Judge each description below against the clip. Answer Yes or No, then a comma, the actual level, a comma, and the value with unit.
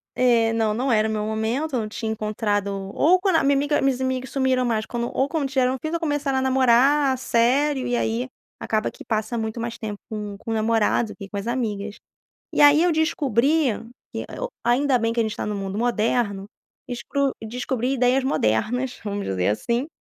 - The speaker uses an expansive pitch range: No, average, 3.6 semitones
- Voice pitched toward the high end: Yes, high, 240 Hz